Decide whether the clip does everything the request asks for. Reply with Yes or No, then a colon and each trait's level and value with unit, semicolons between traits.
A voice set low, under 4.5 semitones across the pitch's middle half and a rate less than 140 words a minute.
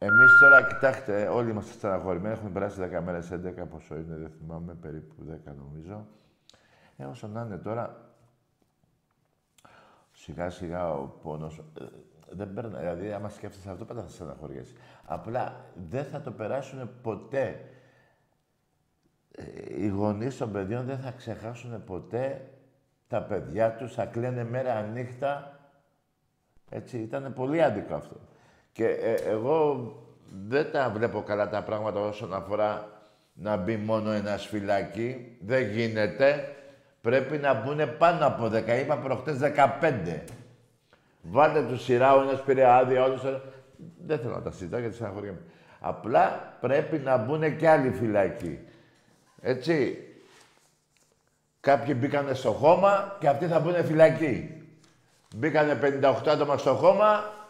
No: low, 125 Hz; average, 5.3 semitones; average, 130 wpm